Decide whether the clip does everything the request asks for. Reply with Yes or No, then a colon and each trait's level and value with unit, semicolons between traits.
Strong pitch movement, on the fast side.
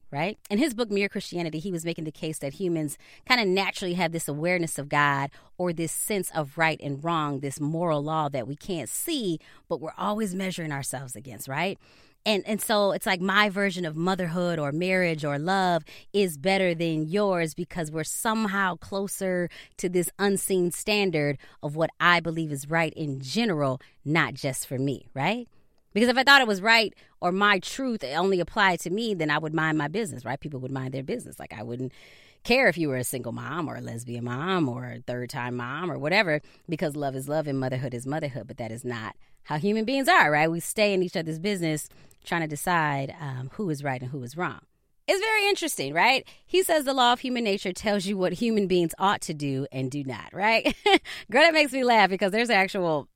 Yes: wide, 5.7 semitones; fast, 215 wpm